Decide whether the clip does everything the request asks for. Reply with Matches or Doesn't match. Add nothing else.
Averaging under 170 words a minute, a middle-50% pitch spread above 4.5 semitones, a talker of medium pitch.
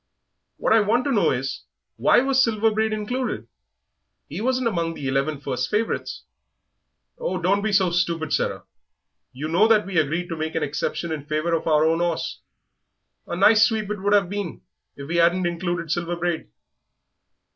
Doesn't match